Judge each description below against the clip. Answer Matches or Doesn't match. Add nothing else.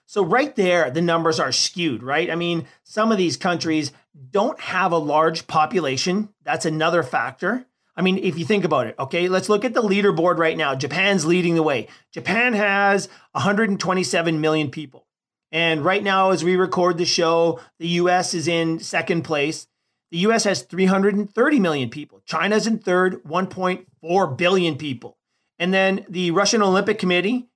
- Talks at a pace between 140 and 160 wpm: Doesn't match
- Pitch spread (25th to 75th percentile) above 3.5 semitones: Doesn't match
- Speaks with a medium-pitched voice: Matches